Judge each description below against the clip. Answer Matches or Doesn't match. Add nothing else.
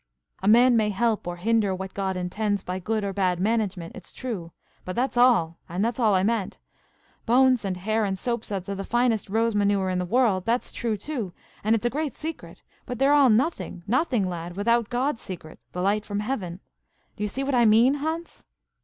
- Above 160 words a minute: Matches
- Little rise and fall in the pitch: Doesn't match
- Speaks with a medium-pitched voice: Doesn't match